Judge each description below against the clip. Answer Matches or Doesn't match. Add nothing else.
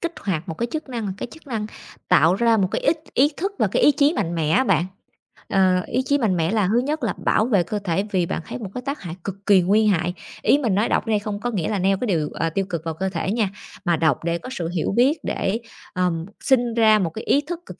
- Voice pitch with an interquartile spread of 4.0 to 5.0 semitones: Doesn't match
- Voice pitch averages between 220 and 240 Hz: Doesn't match